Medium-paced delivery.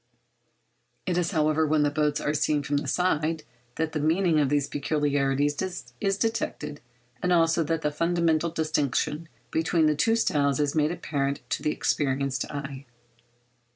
Yes: average, 155 wpm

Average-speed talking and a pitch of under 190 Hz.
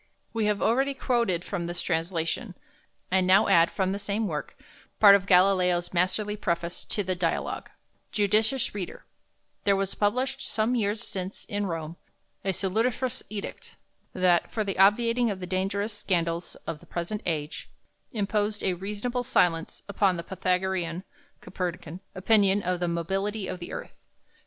No: average, 150 wpm; high, 195 Hz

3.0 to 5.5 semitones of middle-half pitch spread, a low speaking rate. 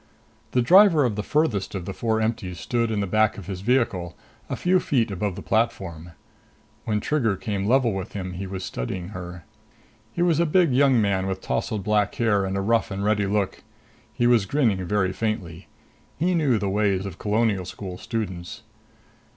No: average, 3.8 semitones; average, 190 wpm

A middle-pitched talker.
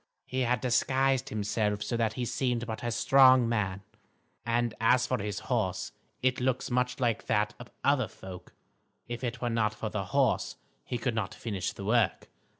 No: low, 115 Hz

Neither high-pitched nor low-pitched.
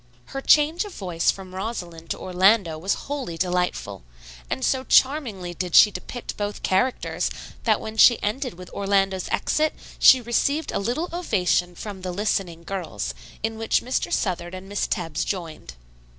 No: high, 195 Hz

